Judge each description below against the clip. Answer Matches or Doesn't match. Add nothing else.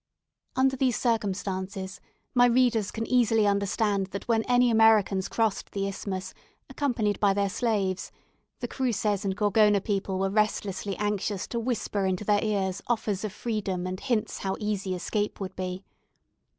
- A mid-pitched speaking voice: Doesn't match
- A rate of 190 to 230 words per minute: Doesn't match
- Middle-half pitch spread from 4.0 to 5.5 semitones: Doesn't match